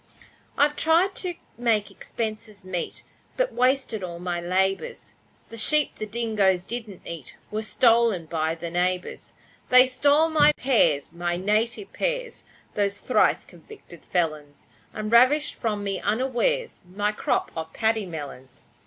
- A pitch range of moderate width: No, wide, 6.2 semitones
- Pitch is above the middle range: Yes, high, 215 Hz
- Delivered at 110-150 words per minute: Yes, slow, 135 wpm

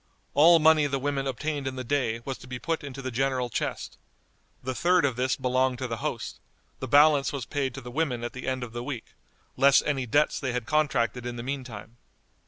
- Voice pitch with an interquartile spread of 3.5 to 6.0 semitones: No, narrow, 2.6 semitones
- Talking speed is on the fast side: Yes, fast, 225 wpm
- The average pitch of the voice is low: Yes, low, 130 Hz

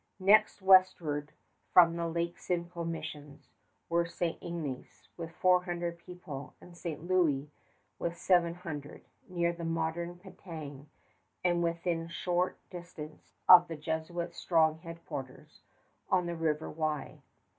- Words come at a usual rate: No, slow, 125 wpm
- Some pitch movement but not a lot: No, narrow, 1.7 semitones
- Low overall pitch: No, medium, 170 Hz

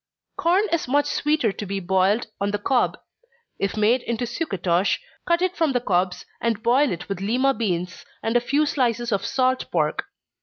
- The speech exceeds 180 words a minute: Yes, average, 190 wpm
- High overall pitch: Yes, high, 235 Hz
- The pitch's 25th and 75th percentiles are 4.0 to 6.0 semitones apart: Yes, wide, 5.6 semitones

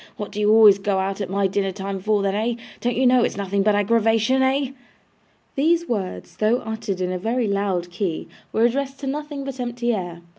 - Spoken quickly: Yes, fast, 215 wpm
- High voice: Yes, high, 215 Hz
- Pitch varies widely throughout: No, average, 4.0 semitones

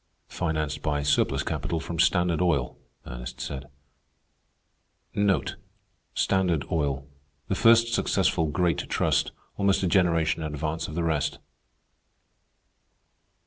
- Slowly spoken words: Yes, slow, 95 wpm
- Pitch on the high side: No, very low, 80 Hz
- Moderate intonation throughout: Yes, average, 3.3 semitones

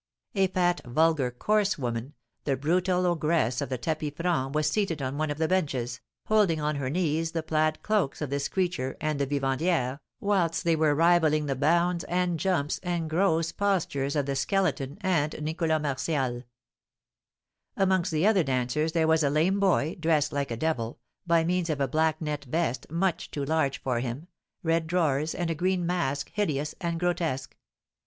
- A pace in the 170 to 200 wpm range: Yes, average, 175 wpm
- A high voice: No, medium, 160 Hz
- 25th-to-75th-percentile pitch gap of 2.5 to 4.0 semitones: Yes, average, 3.7 semitones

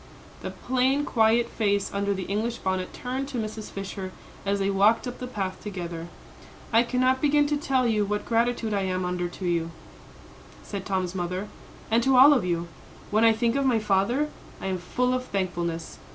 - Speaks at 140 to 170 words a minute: No, average, 190 wpm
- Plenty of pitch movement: No, average, 4.8 semitones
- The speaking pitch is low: No, high, 210 Hz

